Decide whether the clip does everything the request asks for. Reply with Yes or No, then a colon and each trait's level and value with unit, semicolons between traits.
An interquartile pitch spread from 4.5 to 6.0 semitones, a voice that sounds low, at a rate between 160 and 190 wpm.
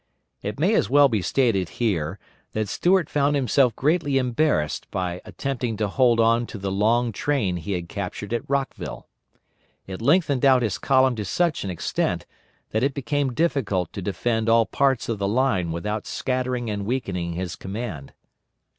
Yes: wide, 5.5 semitones; low, 115 Hz; average, 170 wpm